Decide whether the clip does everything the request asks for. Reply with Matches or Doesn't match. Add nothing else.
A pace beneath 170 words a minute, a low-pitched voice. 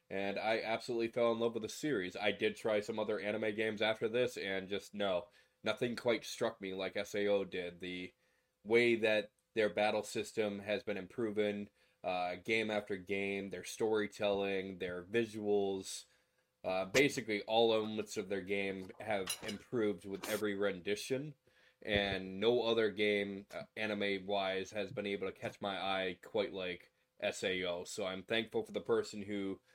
Matches